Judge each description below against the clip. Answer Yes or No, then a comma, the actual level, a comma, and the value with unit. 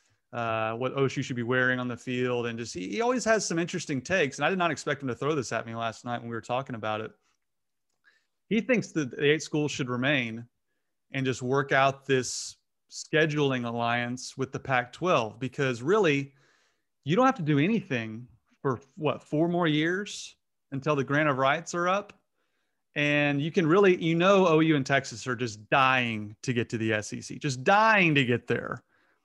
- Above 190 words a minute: Yes, average, 200 wpm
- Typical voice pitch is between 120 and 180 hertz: Yes, low, 135 Hz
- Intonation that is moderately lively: Yes, average, 4.3 semitones